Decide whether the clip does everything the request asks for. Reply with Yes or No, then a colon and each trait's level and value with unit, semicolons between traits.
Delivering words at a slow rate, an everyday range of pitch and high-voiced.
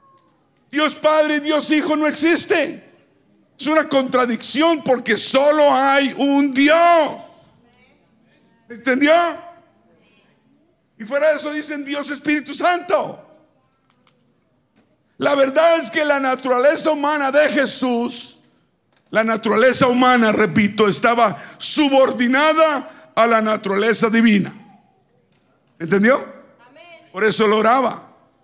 Yes: slow, 100 wpm; average, 4.7 semitones; very high, 275 Hz